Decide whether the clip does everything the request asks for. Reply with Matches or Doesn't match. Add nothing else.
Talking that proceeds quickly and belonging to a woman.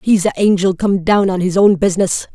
Matches